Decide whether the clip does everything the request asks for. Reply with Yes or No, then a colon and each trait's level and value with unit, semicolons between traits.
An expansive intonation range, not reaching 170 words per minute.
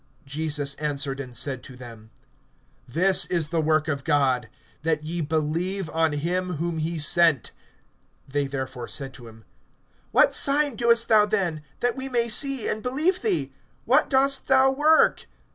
Yes: wide, 7.9 semitones; average, 160 wpm